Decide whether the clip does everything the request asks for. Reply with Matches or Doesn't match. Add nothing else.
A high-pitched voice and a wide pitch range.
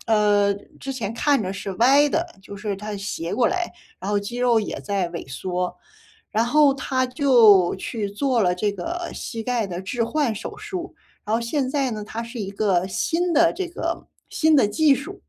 Matches